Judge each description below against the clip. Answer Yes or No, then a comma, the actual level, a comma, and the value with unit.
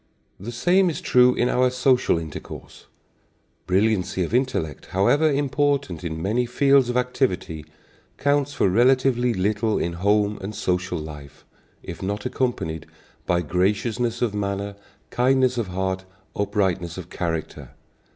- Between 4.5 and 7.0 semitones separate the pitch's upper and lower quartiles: Yes, wide, 5.6 semitones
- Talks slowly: Yes, slow, 130 wpm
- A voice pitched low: Yes, low, 105 Hz